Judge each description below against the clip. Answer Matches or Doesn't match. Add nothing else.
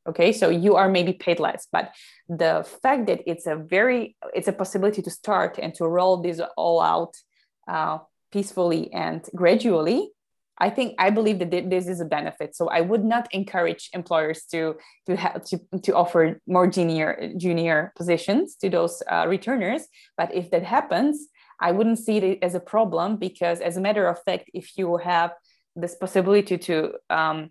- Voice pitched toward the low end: Doesn't match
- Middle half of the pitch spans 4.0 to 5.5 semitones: Doesn't match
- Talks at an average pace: Matches